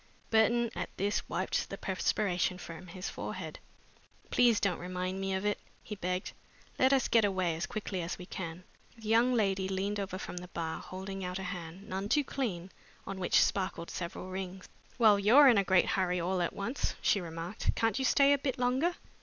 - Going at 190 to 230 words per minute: Yes, average, 195 wpm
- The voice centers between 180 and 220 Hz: Yes, high, 190 Hz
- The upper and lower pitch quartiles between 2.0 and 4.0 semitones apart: Yes, average, 3.4 semitones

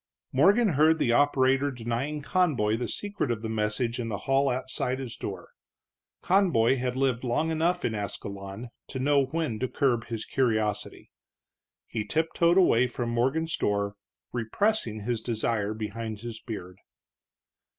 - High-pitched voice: No, low, 125 Hz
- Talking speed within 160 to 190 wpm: No, average, 145 wpm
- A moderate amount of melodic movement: Yes, average, 4.5 semitones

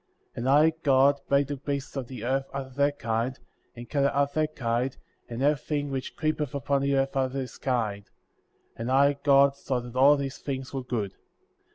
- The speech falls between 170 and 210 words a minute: Yes, average, 190 wpm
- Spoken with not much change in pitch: Yes, narrow, 1.8 semitones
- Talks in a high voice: No, low, 135 Hz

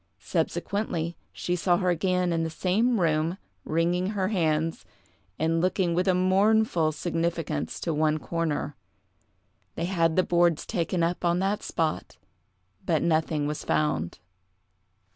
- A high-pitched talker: No, medium, 170 Hz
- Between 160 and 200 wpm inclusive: No, slow, 135 wpm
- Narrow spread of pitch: Yes, narrow, 2.3 semitones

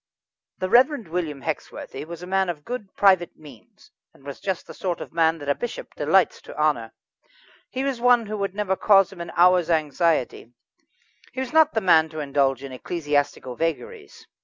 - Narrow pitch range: No, average, 5.2 semitones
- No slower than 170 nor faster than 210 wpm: Yes, average, 185 wpm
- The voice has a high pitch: No, medium, 170 Hz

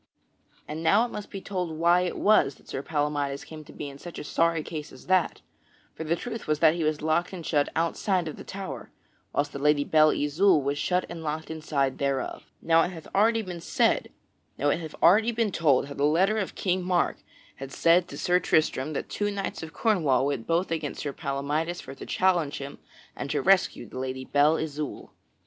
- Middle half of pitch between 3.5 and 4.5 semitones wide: Yes, average, 3.8 semitones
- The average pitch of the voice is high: No, medium, 160 Hz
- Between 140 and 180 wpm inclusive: No, average, 200 wpm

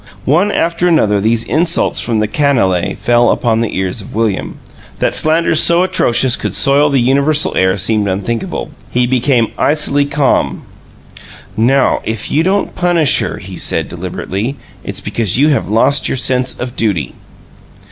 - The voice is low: Yes, low, 125 Hz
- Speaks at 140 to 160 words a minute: Yes, average, 155 wpm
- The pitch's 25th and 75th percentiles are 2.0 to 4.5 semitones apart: No, average, 5.2 semitones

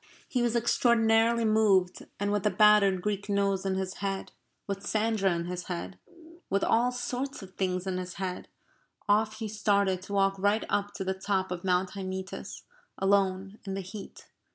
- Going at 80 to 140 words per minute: No, average, 175 wpm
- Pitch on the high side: Yes, high, 195 Hz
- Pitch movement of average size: No, narrow, 2.2 semitones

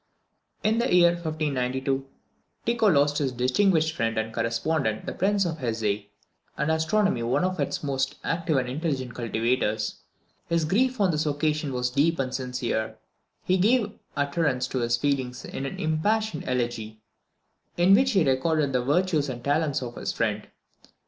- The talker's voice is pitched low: No, medium, 145 Hz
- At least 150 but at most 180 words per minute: Yes, average, 160 wpm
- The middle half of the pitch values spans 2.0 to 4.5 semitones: No, average, 5.1 semitones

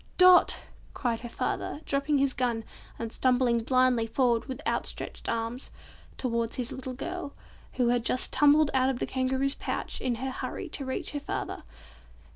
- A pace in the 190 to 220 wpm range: No, average, 165 wpm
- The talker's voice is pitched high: Yes, very high, 255 Hz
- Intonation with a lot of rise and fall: No, narrow, 2.4 semitones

